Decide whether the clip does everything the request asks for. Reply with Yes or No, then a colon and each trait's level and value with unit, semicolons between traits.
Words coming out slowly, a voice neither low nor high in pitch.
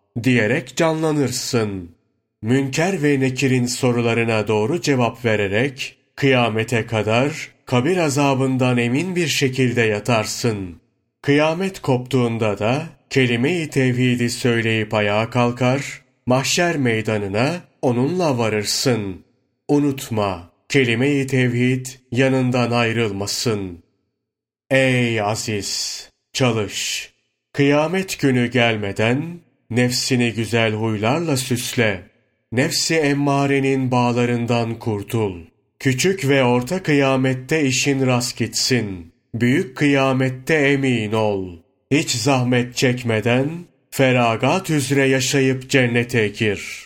No: slow, 85 wpm; low, 125 Hz